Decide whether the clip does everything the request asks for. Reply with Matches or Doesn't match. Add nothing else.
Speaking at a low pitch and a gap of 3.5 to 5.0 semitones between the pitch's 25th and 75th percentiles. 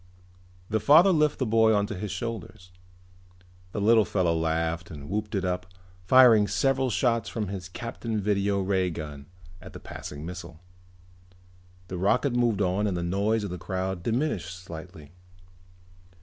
Matches